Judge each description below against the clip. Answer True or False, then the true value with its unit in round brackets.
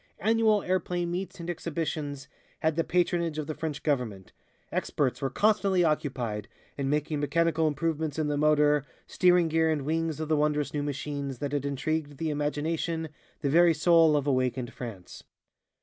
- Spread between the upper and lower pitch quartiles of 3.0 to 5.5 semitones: False (2.5 semitones)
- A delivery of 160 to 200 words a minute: True (165 wpm)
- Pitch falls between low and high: True (150 Hz)